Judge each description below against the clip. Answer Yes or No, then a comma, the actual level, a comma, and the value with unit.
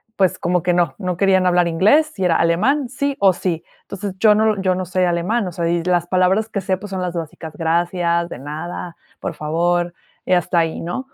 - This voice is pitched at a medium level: Yes, medium, 180 Hz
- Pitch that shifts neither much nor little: No, narrow, 2.3 semitones